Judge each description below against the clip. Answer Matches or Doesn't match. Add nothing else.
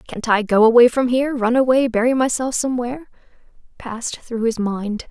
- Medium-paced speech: Matches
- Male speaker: Doesn't match